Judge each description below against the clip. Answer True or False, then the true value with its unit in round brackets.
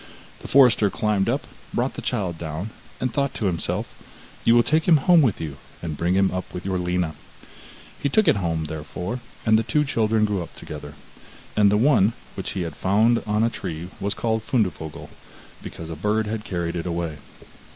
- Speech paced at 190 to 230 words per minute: True (195 wpm)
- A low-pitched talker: True (100 Hz)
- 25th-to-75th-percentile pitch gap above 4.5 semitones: True (5.0 semitones)